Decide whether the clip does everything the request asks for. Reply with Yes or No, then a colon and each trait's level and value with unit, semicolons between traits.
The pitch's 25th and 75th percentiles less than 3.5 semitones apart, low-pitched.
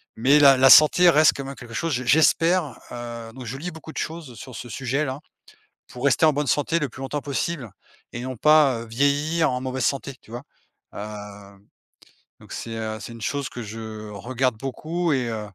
No: average, 4.2 semitones; low, 130 Hz